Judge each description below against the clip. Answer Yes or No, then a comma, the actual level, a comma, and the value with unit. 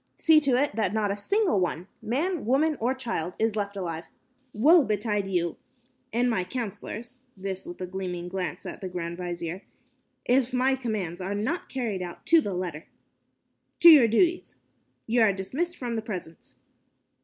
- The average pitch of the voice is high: Yes, high, 215 Hz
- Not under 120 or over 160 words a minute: No, average, 175 wpm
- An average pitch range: No, wide, 5.9 semitones